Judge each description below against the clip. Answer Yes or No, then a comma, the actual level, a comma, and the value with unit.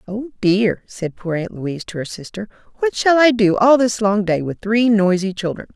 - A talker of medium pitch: No, high, 205 Hz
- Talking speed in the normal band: No, fast, 220 wpm